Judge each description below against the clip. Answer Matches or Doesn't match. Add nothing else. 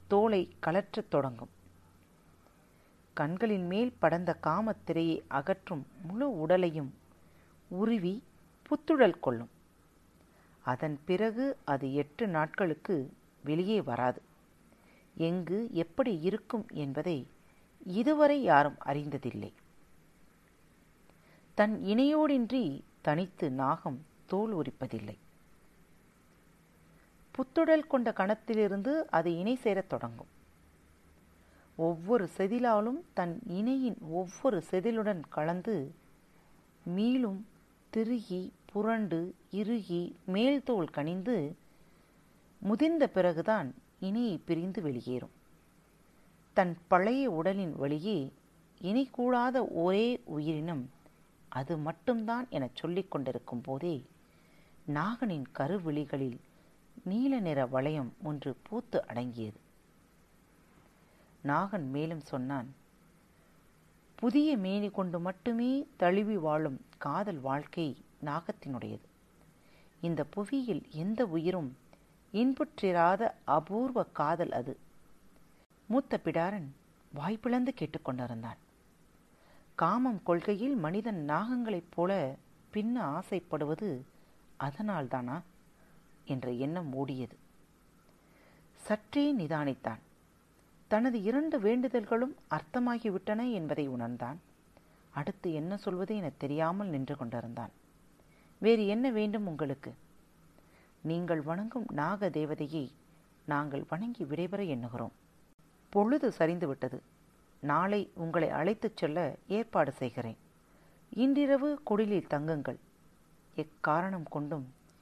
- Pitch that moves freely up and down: Matches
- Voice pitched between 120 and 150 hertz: Doesn't match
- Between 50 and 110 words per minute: Matches